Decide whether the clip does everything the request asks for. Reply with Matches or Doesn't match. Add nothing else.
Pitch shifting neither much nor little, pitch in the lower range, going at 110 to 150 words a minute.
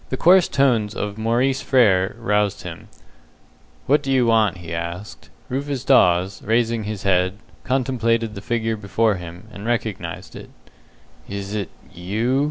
Matches